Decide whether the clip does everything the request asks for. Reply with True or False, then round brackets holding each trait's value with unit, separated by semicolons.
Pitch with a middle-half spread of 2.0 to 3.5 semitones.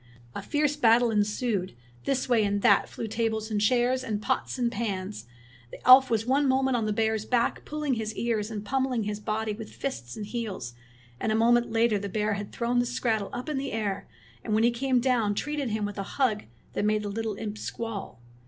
True (2.8 semitones)